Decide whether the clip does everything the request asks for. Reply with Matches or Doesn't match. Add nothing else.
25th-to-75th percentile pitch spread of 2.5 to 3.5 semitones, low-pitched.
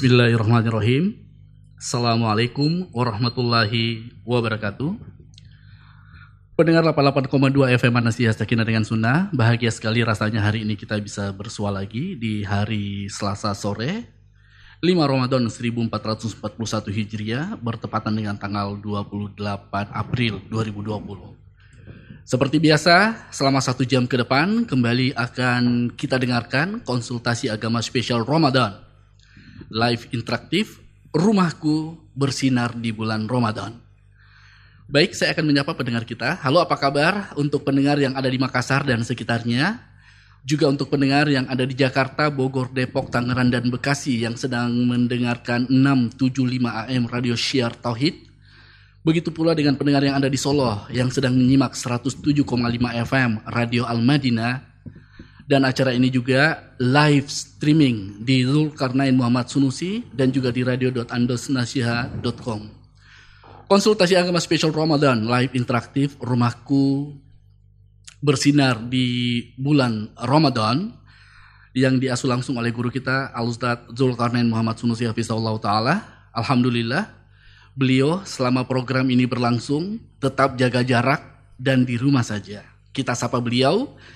Matches